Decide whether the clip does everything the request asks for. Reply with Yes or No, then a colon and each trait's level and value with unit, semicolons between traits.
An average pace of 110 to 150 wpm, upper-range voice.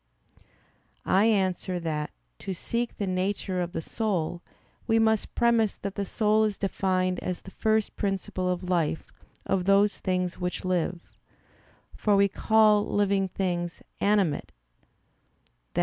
Yes: slow, 135 wpm; high, 195 Hz